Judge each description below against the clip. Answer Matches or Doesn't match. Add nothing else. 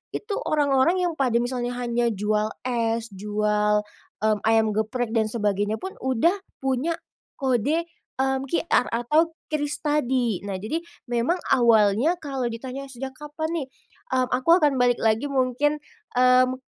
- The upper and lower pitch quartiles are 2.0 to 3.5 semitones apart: Doesn't match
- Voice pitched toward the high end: Matches